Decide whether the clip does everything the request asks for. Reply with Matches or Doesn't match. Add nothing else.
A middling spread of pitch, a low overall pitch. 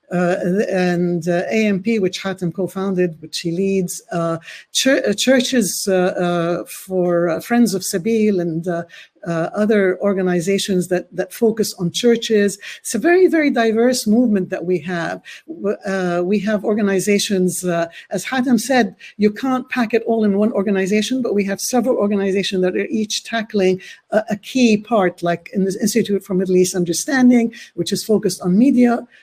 Doesn't match